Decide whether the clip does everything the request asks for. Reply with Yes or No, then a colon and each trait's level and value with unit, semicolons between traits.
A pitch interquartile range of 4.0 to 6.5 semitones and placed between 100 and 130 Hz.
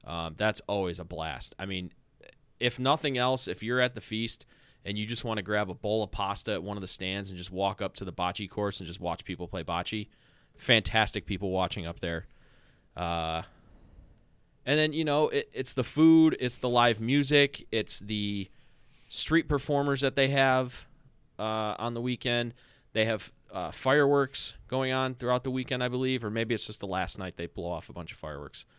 Yes: average, 5.3 semitones; low, 110 Hz